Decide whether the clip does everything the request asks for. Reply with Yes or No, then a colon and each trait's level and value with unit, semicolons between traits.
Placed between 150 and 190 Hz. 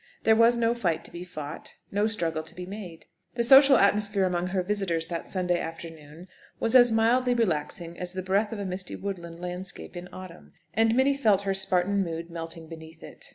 Yes: medium, 185 Hz